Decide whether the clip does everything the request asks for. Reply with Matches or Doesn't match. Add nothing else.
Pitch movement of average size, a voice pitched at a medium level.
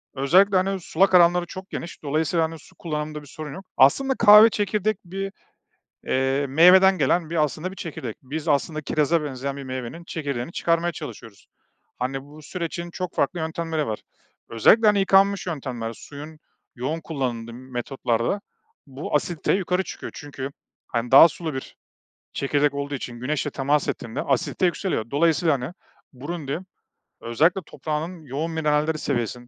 Matches